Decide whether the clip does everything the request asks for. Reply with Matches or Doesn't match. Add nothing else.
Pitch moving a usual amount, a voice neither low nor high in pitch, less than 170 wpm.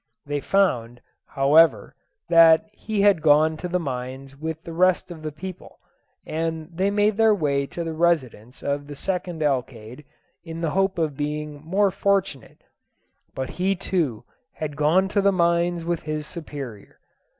Matches